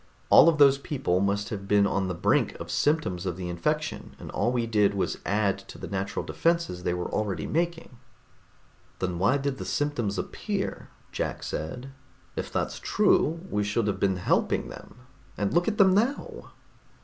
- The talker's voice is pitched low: Yes, low, 105 Hz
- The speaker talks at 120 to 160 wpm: No, average, 180 wpm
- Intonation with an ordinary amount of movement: No, wide, 7.6 semitones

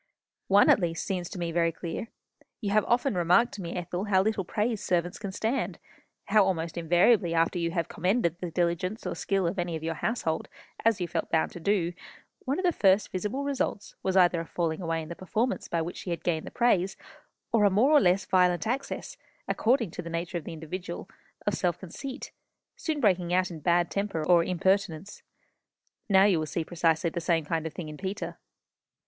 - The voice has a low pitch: No, medium, 180 Hz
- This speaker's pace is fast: Yes, fast, 210 wpm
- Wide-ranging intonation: No, average, 3.4 semitones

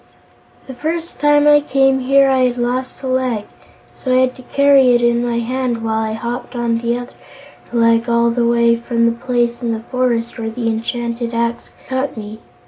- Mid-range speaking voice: No, high, 240 Hz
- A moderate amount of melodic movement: No, narrow, 1.8 semitones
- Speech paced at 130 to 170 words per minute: No, average, 200 wpm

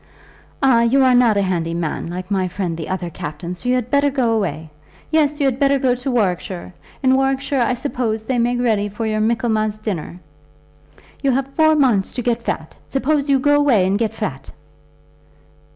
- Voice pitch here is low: No, high, 235 Hz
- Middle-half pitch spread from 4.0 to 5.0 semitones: No, wide, 5.5 semitones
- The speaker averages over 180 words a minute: Yes, average, 195 wpm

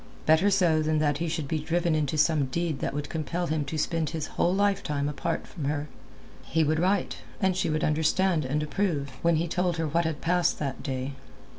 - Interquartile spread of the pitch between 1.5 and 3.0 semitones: Yes, narrow, 2.5 semitones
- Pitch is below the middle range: No, medium, 160 Hz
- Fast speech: Yes, fast, 210 wpm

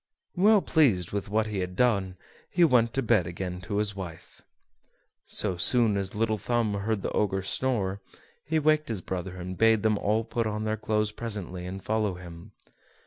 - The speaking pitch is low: Yes, low, 105 Hz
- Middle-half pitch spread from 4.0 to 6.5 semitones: No, average, 3.3 semitones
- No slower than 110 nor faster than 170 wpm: No, average, 185 wpm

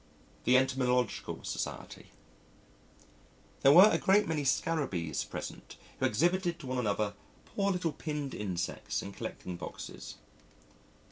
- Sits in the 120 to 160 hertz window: Yes, low, 135 Hz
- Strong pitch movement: Yes, wide, 8.0 semitones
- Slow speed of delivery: Yes, slow, 120 wpm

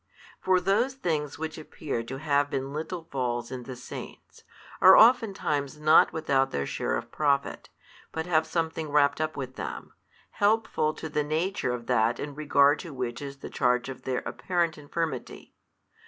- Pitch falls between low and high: Yes, medium, 150 Hz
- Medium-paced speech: Yes, average, 170 wpm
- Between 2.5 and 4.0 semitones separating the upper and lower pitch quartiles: Yes, average, 3.3 semitones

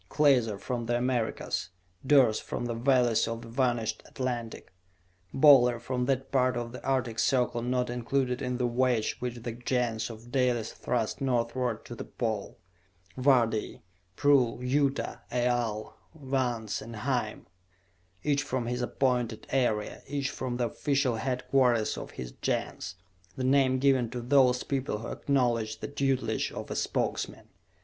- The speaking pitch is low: Yes, low, 125 Hz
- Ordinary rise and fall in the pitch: No, narrow, 2.0 semitones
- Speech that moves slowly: No, average, 145 wpm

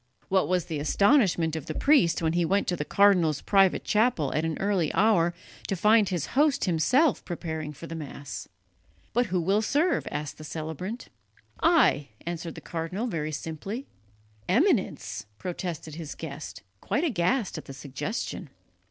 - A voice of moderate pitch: Yes, medium, 175 Hz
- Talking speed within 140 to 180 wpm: Yes, average, 160 wpm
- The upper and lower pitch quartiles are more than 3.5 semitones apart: Yes, average, 5.0 semitones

